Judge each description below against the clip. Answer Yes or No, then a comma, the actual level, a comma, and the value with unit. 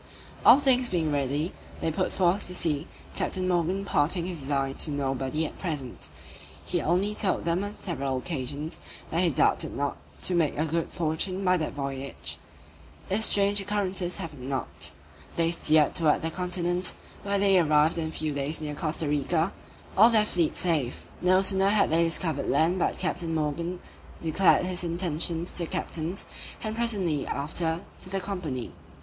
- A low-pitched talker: No, medium, 170 Hz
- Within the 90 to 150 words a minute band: No, average, 170 wpm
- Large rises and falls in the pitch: No, average, 3.6 semitones